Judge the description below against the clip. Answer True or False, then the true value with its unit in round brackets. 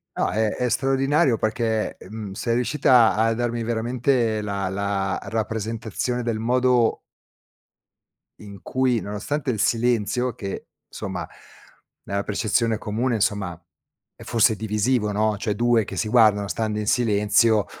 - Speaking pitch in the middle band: False (110 Hz)